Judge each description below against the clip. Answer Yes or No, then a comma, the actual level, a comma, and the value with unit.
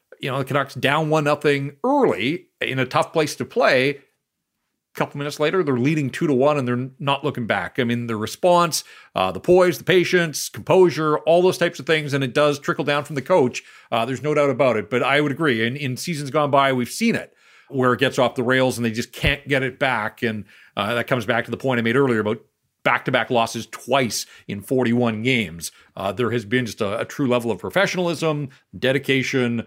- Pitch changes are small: No, average, 3.9 semitones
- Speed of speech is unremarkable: No, fast, 230 wpm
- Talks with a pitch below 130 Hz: No, low, 135 Hz